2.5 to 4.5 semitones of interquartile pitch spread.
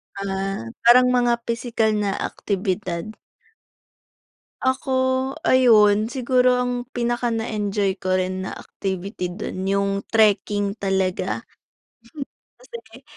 Yes: average, 4.2 semitones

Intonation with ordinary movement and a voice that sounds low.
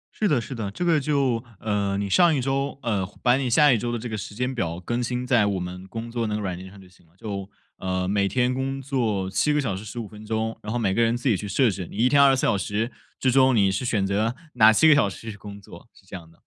Yes: average, 4.4 semitones; low, 110 Hz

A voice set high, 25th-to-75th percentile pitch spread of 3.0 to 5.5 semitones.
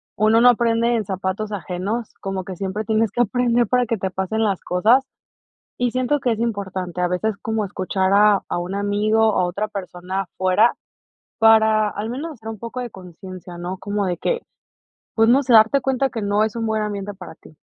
Yes: high, 210 Hz; average, 3.3 semitones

